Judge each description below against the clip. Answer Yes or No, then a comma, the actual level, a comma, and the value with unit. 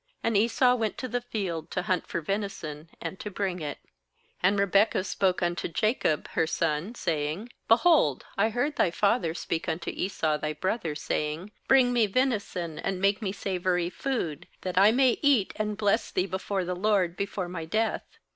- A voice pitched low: No, high, 195 Hz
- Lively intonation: No, average, 4.4 semitones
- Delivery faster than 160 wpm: Yes, average, 175 wpm